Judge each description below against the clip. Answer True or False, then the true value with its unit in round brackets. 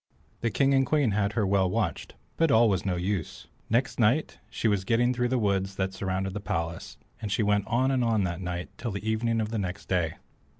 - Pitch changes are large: False (3.8 semitones)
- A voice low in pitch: True (105 Hz)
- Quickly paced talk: True (225 wpm)